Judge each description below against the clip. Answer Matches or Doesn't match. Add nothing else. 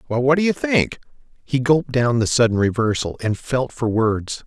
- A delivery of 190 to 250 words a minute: Matches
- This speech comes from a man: Matches